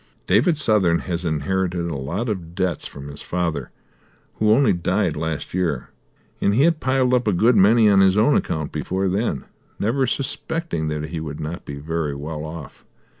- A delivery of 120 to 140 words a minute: No, average, 180 wpm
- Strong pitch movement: Yes, wide, 5.7 semitones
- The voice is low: Yes, very low, 90 Hz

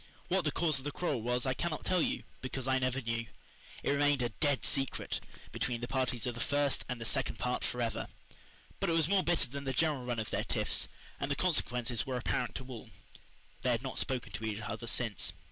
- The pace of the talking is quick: Yes, fast, 215 wpm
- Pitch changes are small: No, average, 3.2 semitones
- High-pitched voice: No, low, 130 Hz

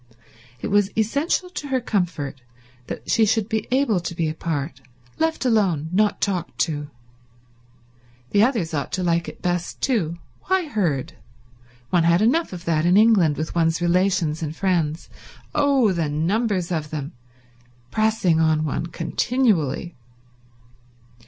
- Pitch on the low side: No, medium, 175 Hz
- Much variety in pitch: Yes, wide, 5.8 semitones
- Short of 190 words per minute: Yes, slow, 135 wpm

